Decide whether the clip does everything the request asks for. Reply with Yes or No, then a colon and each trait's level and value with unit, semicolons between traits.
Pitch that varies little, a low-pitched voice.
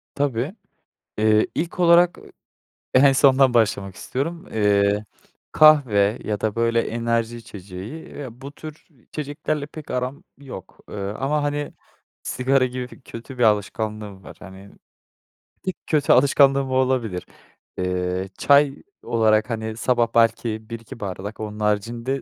No: average, 4.5 semitones; low, 115 Hz